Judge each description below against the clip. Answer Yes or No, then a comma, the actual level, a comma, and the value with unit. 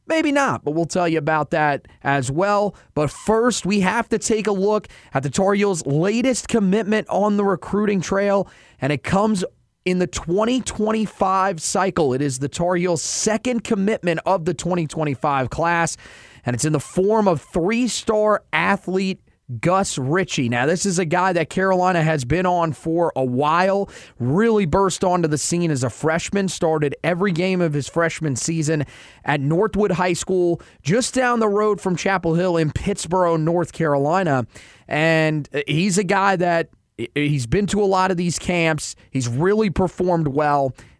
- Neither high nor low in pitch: Yes, medium, 175 Hz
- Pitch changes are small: No, average, 4.7 semitones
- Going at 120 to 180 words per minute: Yes, average, 170 wpm